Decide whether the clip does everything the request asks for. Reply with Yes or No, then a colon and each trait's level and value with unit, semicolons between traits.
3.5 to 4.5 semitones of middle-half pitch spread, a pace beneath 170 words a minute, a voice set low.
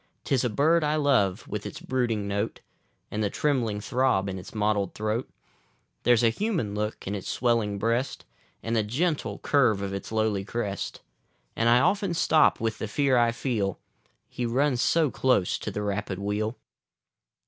No: average, 4.1 semitones; average, 175 wpm; low, 115 Hz